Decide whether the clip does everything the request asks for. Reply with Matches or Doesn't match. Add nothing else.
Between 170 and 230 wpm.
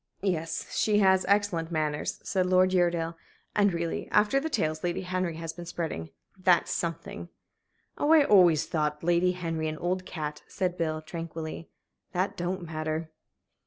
Doesn't match